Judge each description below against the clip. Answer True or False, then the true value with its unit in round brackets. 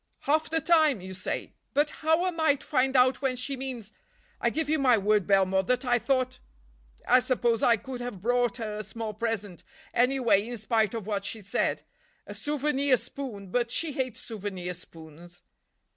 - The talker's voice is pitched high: True (240 Hz)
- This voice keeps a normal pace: True (175 wpm)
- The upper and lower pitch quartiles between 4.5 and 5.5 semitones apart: True (4.9 semitones)